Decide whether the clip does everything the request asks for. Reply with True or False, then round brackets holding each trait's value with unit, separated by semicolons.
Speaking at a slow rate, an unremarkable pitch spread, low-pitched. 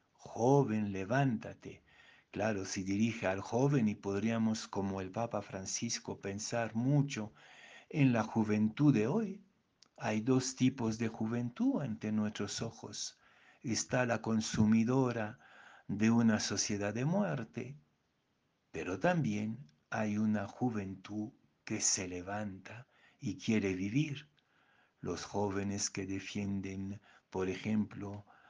True (110 wpm; 3.2 semitones; 110 Hz)